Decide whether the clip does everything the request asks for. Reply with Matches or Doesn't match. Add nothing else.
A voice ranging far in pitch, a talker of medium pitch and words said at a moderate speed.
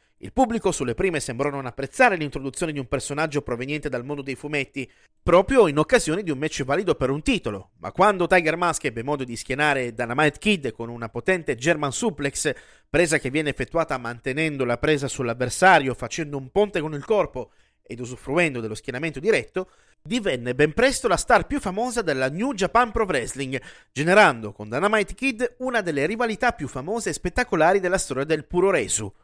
Doesn't match